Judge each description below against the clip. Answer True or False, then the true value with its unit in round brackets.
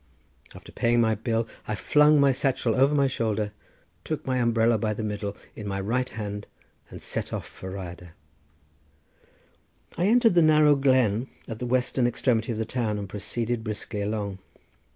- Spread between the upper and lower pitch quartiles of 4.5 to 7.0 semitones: False (3.9 semitones)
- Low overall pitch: True (115 Hz)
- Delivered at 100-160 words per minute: False (170 wpm)